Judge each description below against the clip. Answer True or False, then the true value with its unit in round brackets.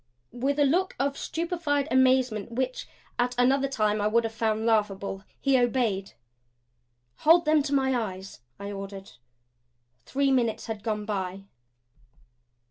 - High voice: True (245 Hz)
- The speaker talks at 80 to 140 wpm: True (135 wpm)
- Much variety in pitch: False (4.6 semitones)